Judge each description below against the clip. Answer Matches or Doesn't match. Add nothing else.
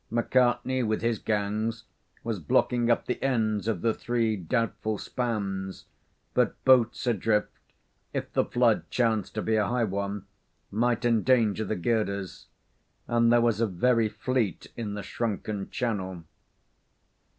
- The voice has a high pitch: Doesn't match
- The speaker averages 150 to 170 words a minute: Doesn't match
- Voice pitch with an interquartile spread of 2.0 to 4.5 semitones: Matches